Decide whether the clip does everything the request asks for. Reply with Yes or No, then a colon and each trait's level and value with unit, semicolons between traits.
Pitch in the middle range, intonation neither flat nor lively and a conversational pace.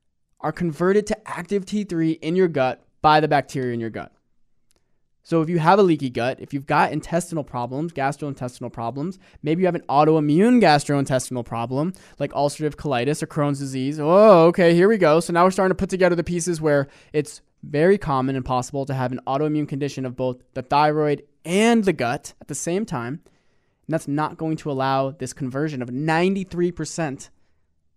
Yes: medium, 150 Hz; average, 4.2 semitones; average, 185 wpm